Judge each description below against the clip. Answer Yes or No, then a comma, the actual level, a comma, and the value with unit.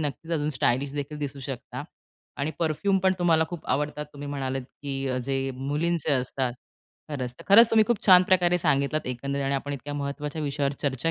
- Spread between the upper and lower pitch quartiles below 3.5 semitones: Yes, average, 2.9 semitones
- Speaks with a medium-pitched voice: Yes, medium, 145 Hz